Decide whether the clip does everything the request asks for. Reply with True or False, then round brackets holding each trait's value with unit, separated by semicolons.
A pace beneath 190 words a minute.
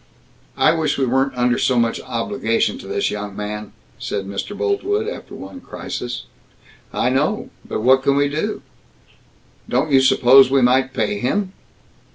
True (160 wpm)